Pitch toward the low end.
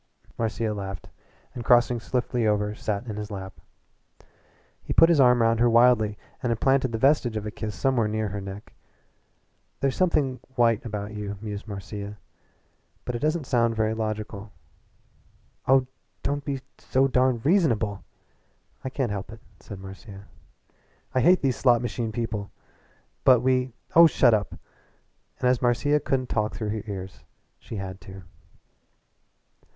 Yes: low, 115 Hz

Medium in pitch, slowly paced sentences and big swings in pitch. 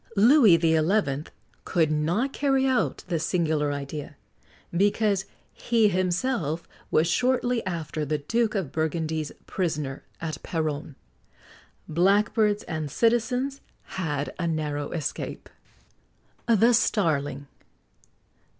Yes: medium, 170 Hz; slow, 105 wpm; wide, 6.1 semitones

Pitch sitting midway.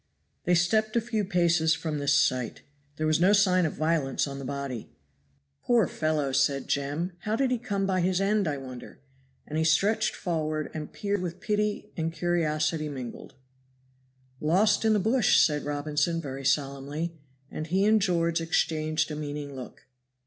Yes: medium, 160 Hz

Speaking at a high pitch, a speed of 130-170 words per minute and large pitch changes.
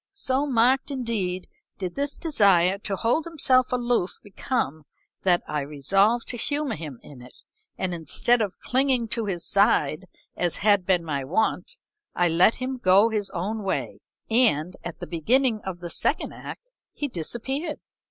Yes: high, 205 Hz; average, 160 wpm; wide, 6.3 semitones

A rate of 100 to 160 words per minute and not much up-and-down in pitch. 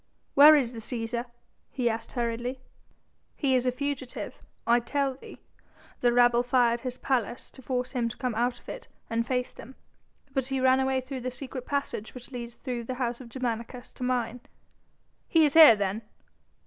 No: average, 185 wpm; narrow, 1.9 semitones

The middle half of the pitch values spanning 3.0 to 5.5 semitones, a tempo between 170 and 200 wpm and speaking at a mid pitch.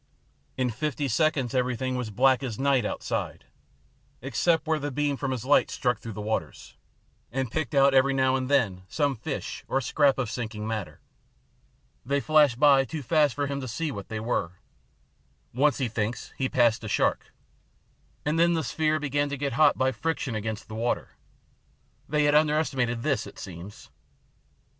No: average, 3.8 semitones; average, 175 wpm; low, 130 Hz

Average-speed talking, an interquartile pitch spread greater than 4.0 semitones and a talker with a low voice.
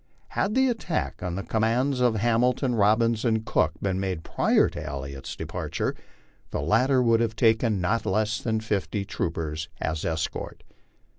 Yes: average, 155 wpm; average, 4.6 semitones; low, 110 Hz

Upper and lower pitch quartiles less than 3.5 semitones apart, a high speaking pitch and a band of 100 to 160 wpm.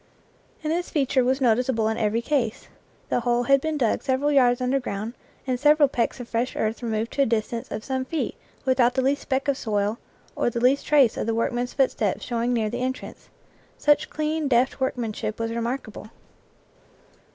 No: average, 2.9 semitones; high, 245 Hz; average, 190 wpm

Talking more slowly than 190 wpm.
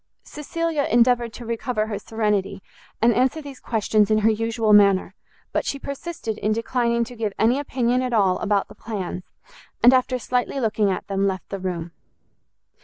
Yes: average, 175 wpm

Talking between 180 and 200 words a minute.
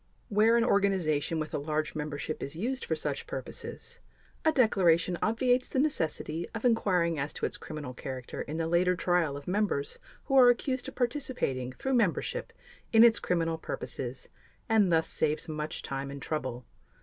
No: average, 170 wpm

